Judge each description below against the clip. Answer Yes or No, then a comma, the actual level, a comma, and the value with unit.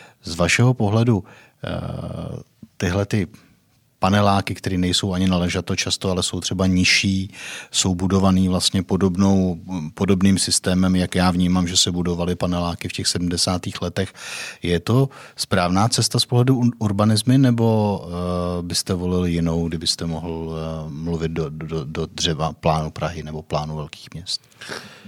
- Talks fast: No, average, 135 wpm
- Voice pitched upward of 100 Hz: No, very low, 90 Hz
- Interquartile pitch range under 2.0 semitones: No, narrow, 2.4 semitones